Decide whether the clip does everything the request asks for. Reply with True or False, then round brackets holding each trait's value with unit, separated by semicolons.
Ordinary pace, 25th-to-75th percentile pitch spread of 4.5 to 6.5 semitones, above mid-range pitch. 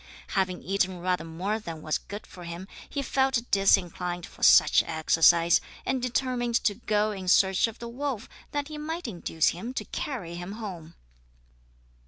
True (165 wpm; 5.6 semitones; 195 Hz)